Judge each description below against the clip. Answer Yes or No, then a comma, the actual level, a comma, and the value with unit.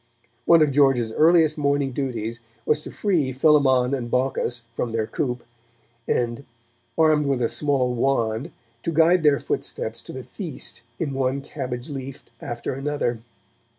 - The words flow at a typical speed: Yes, average, 150 wpm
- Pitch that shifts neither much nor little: Yes, average, 3.3 semitones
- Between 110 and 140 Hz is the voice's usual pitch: Yes, low, 135 Hz